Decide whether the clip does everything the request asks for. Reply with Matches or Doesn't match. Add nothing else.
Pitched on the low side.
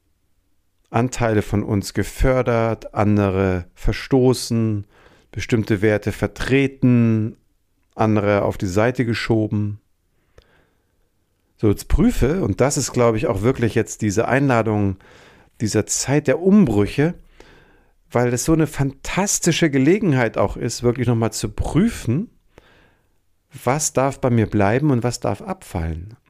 Matches